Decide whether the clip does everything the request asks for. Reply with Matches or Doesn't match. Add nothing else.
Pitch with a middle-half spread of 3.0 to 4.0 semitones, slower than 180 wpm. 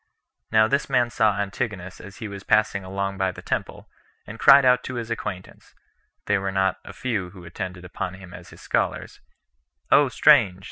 Doesn't match